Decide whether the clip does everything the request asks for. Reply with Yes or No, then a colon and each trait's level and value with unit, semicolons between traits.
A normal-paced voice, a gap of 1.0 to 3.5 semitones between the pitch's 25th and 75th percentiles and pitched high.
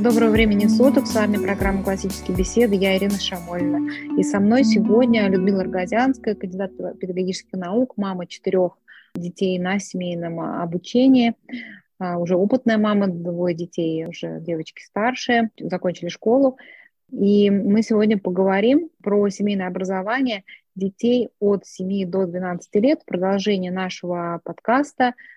No: average, 125 wpm; average, 4.0 semitones; high, 200 Hz